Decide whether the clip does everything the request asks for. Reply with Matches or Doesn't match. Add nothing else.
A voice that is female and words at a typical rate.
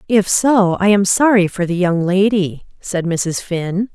Matches